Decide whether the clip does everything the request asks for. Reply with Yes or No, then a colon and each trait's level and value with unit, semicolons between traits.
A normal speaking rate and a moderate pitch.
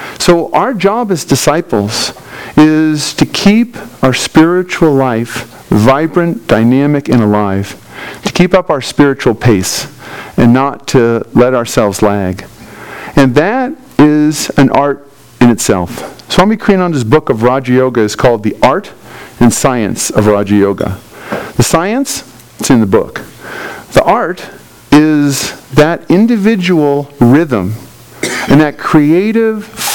No: slow, 130 wpm; medium, 145 Hz